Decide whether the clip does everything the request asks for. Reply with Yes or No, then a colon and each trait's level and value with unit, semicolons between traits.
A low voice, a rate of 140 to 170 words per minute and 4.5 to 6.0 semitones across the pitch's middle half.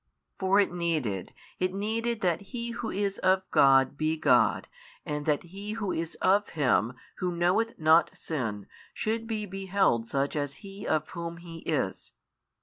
No: medium, 175 Hz; average, 160 wpm; average, 4.9 semitones